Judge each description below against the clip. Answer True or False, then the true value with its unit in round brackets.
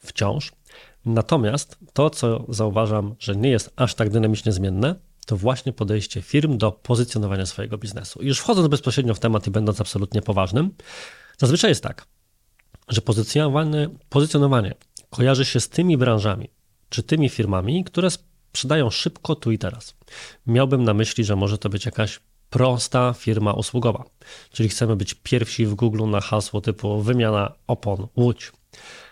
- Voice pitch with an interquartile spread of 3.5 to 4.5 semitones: True (4.0 semitones)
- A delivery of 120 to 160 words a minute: True (145 wpm)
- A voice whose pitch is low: True (115 Hz)